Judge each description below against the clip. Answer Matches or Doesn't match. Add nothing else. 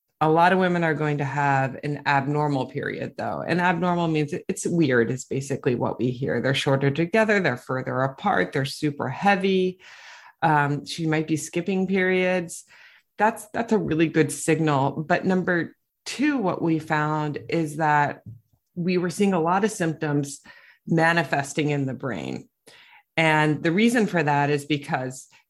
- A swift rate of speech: Doesn't match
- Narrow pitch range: Doesn't match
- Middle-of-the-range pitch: Matches